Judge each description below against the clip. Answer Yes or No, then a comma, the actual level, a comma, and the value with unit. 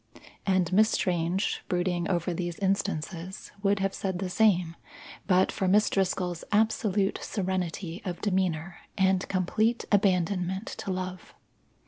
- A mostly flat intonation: Yes, narrow, 1.9 semitones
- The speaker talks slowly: Yes, slow, 125 wpm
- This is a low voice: No, medium, 185 Hz